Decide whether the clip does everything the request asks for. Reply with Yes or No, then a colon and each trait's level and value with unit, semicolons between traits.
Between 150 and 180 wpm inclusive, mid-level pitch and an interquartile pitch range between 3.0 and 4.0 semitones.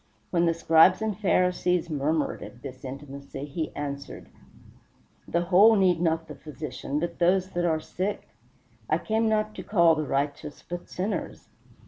Yes: average, 155 wpm; medium, 170 Hz; average, 3.6 semitones